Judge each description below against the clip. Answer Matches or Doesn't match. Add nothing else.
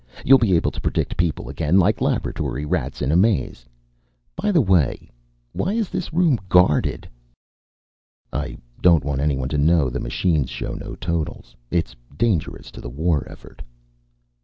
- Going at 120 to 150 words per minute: Doesn't match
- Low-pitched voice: Matches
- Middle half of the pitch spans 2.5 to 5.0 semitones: Doesn't match